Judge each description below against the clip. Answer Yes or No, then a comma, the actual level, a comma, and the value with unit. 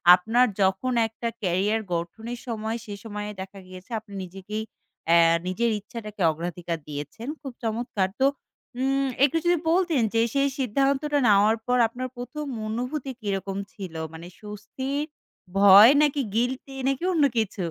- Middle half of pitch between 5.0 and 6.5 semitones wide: Yes, average, 5.3 semitones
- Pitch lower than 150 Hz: No, high, 220 Hz